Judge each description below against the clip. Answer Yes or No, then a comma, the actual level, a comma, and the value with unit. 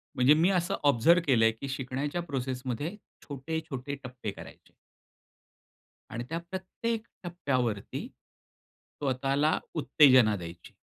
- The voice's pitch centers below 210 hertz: Yes, low, 135 Hz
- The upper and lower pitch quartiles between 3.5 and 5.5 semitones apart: Yes, average, 4.5 semitones